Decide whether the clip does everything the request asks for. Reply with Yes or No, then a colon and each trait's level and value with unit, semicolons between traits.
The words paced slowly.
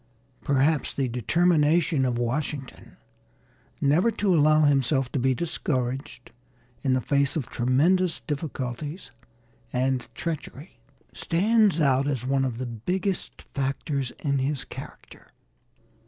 Yes: slow, 115 wpm